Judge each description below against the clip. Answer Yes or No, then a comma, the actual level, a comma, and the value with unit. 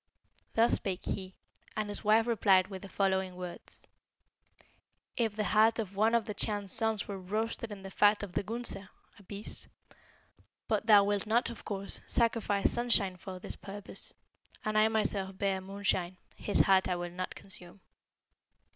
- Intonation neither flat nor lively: No, narrow, 2.3 semitones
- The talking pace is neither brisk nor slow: Yes, average, 165 wpm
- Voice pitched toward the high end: Yes, high, 200 Hz